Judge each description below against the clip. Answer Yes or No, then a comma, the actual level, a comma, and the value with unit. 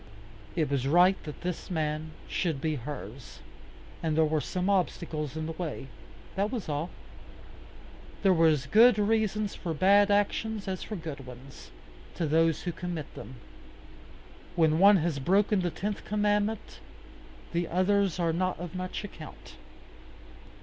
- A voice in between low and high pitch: Yes, medium, 175 Hz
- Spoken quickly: No, average, 150 wpm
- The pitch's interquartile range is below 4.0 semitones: No, average, 4.3 semitones